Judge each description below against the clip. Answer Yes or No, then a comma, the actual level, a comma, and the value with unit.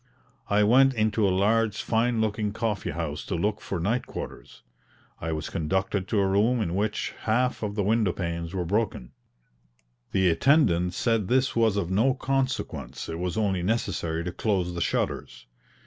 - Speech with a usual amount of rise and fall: Yes, average, 4.2 semitones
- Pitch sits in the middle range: No, low, 100 Hz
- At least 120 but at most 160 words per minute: No, average, 170 wpm